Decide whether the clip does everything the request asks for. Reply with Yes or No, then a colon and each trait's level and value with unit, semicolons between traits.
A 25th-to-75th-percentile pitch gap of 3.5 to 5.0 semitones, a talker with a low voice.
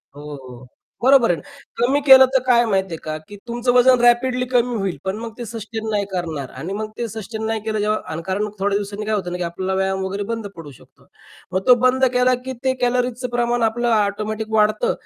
No: average, 4.0 semitones; high, 215 Hz